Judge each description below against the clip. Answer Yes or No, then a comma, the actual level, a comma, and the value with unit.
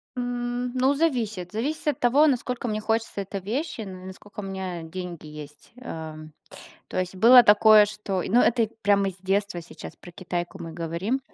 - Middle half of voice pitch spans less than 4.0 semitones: No, average, 5.2 semitones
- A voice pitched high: Yes, high, 205 Hz